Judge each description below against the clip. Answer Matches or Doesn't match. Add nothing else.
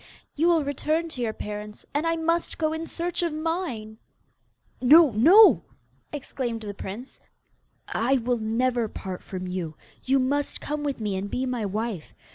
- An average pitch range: Doesn't match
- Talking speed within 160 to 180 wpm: Matches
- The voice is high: Matches